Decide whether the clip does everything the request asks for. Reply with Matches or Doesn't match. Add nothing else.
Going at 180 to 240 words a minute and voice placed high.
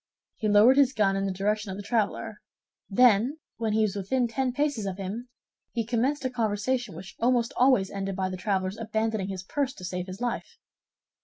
Matches